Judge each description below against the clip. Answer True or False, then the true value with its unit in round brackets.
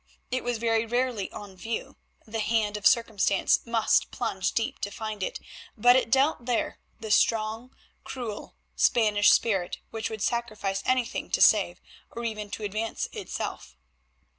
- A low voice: False (225 Hz)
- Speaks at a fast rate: False (150 wpm)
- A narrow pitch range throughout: True (2.2 semitones)